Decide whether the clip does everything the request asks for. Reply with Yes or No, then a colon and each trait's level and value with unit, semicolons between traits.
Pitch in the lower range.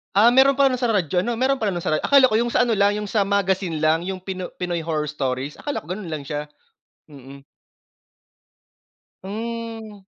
No: high, 195 Hz